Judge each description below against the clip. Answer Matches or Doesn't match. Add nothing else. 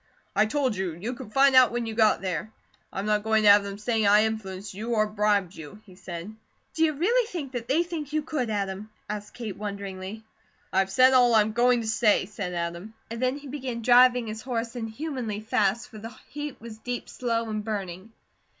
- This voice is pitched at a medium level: Doesn't match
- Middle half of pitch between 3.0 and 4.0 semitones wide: Matches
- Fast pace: Matches